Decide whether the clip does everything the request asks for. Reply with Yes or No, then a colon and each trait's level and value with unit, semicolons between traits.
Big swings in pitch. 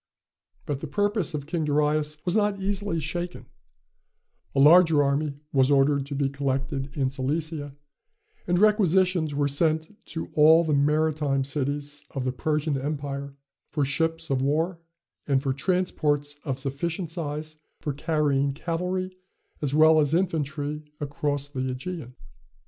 No: average, 2.7 semitones